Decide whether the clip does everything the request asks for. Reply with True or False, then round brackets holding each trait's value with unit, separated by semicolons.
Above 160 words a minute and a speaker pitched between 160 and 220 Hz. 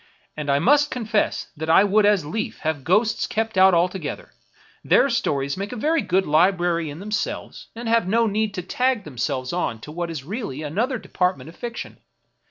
True (185 wpm; 190 Hz)